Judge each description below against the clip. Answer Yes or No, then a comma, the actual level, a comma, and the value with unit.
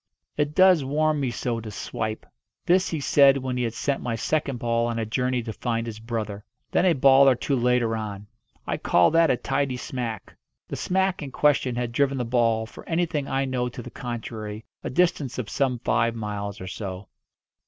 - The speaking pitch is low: Yes, low, 125 Hz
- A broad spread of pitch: No, average, 3.6 semitones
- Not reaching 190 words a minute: No, fast, 205 wpm